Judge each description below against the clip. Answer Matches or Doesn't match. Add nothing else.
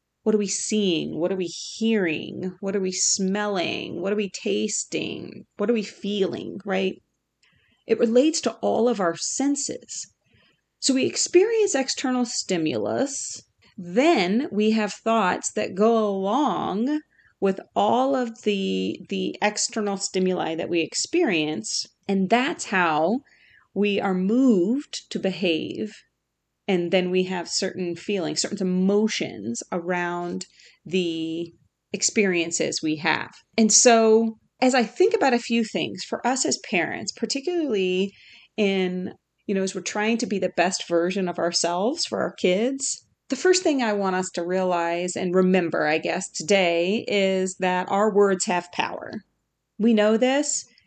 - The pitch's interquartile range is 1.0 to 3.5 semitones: Doesn't match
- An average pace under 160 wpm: Matches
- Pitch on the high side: Matches